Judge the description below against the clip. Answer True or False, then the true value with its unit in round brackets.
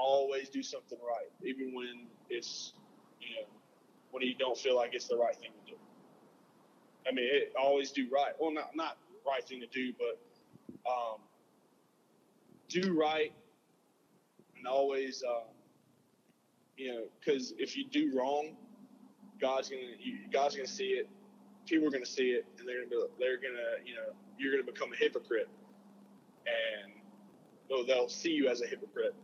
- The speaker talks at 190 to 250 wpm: False (165 wpm)